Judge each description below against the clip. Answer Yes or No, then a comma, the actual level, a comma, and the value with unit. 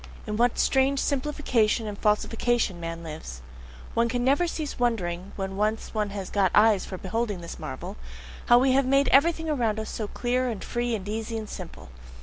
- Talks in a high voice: Yes, high, 225 Hz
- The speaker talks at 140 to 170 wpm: No, average, 180 wpm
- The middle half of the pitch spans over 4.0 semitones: Yes, average, 4.4 semitones